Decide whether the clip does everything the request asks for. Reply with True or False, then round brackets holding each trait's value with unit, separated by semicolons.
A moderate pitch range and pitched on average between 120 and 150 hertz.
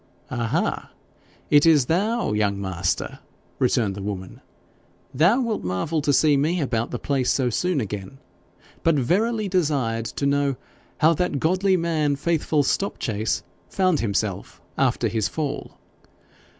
False (6.8 semitones; 140 Hz)